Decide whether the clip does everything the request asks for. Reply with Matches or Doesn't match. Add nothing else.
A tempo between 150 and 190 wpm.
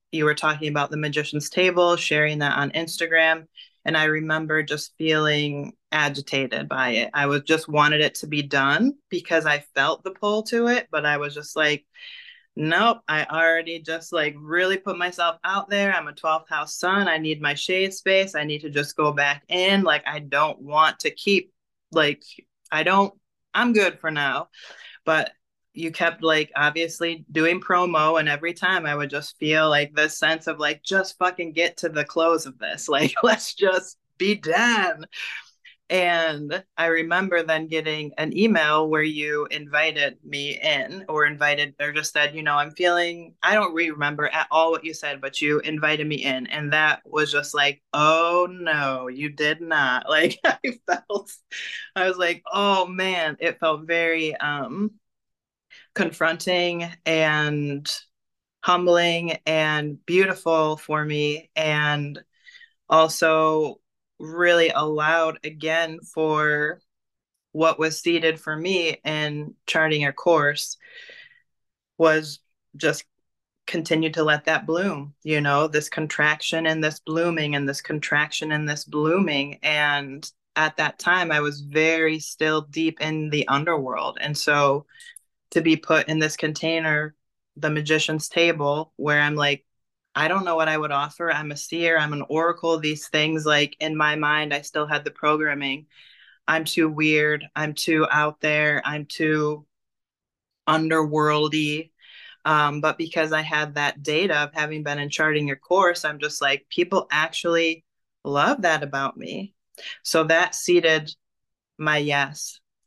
Matches